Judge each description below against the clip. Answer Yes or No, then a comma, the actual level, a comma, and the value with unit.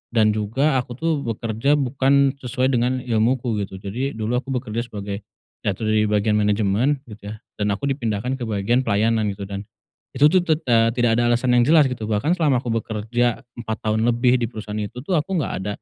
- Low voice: Yes, low, 115 Hz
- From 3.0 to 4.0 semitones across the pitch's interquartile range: Yes, average, 3.5 semitones